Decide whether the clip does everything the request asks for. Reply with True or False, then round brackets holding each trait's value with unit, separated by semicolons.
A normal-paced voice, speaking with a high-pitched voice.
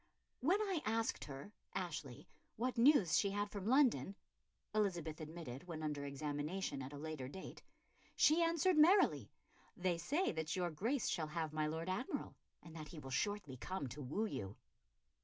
False (165 wpm; 170 Hz)